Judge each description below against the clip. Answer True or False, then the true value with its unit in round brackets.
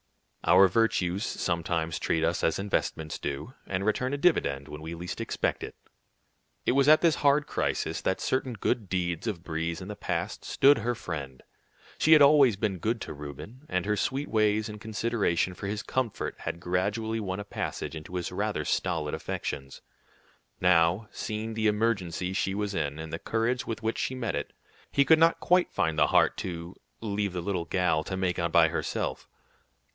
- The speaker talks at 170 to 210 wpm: True (185 wpm)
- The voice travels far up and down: False (5.0 semitones)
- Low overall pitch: True (95 Hz)